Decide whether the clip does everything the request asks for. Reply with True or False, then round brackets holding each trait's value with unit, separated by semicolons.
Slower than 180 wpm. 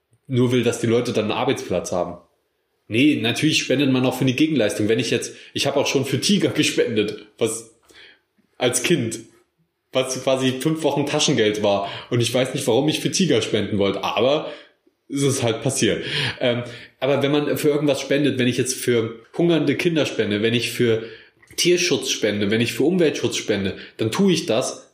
False (190 wpm)